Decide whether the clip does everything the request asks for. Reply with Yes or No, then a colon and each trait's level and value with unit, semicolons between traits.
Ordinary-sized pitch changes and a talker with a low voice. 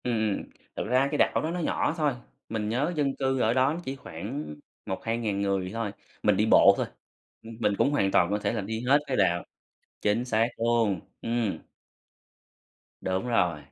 Yes: average, 4.5 semitones; low, 115 Hz